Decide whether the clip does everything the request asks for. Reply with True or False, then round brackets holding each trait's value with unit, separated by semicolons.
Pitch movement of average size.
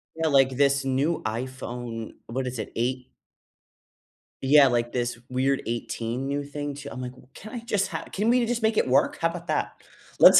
True (3.8 semitones)